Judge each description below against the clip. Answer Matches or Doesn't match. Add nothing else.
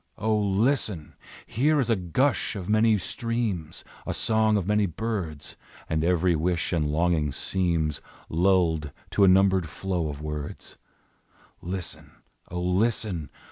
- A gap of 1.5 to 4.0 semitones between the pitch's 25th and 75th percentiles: Doesn't match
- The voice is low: Matches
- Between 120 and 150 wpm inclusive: Matches